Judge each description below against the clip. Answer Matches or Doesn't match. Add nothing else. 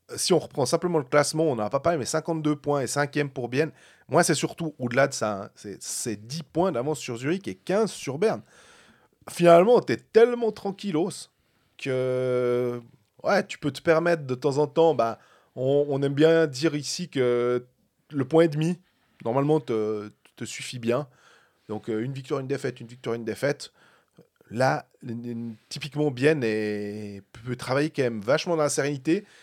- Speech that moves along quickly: Doesn't match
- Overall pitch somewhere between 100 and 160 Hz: Matches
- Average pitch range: Matches